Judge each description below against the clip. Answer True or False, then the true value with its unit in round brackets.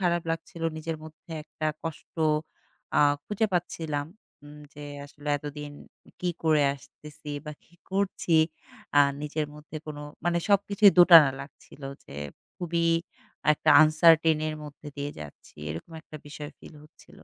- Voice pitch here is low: False (155 Hz)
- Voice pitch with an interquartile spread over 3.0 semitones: False (2.5 semitones)